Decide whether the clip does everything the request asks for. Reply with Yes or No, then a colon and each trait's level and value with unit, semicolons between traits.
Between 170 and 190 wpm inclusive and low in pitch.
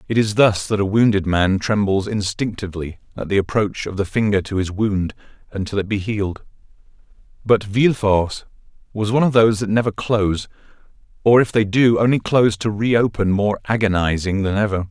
Yes: average, 175 wpm; low, 105 Hz